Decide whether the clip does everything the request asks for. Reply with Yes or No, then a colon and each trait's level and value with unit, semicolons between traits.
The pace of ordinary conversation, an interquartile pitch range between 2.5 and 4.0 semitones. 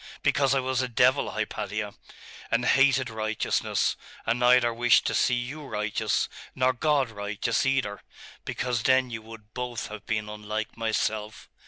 Yes: average, 150 wpm; average, 3.0 semitones